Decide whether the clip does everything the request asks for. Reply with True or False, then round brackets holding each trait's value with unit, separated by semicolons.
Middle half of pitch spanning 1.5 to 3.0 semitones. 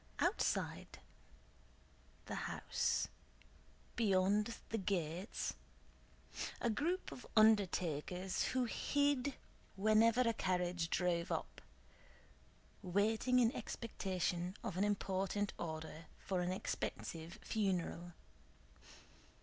False (4.0 semitones)